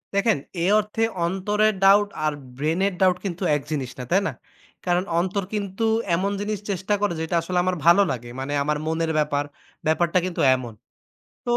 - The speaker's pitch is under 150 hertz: No, medium, 180 Hz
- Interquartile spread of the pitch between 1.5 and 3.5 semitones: No, average, 4.2 semitones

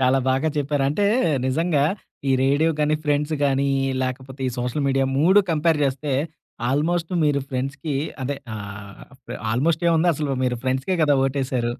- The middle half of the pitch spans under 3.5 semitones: Yes, average, 2.8 semitones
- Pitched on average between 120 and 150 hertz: Yes, medium, 140 Hz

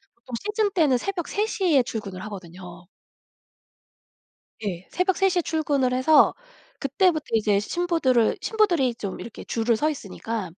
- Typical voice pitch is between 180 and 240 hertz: No, very high, 260 Hz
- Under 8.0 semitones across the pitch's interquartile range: No, wide, 8.4 semitones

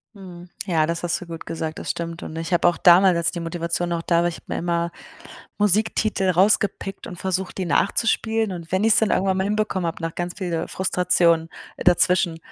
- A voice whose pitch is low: No, medium, 175 Hz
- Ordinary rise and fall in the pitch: No, narrow, 2.2 semitones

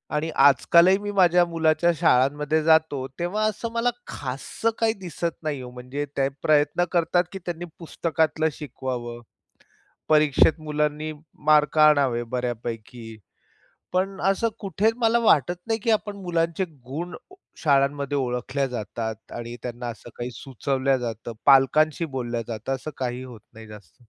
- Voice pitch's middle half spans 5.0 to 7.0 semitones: Yes, average, 5.3 semitones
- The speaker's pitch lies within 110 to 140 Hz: No, medium, 150 Hz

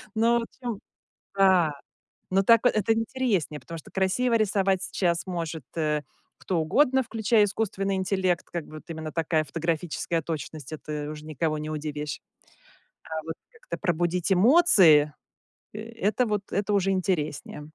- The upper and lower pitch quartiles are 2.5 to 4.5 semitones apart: No, average, 5.2 semitones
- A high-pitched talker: No, medium, 180 Hz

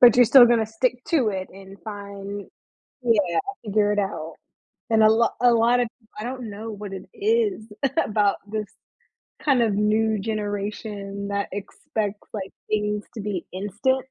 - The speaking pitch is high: Yes, high, 210 Hz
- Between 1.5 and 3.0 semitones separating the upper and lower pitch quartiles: Yes, narrow, 2.5 semitones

